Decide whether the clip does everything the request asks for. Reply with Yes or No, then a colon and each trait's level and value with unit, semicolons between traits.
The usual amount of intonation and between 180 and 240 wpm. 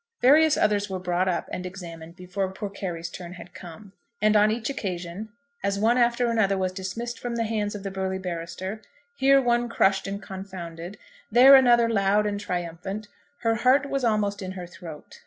Yes: average, 3.8 semitones; average, 185 wpm